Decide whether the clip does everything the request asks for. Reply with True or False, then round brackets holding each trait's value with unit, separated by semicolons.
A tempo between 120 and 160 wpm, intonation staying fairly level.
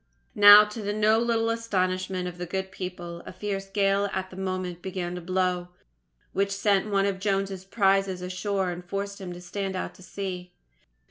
False (185 wpm; 1.7 semitones)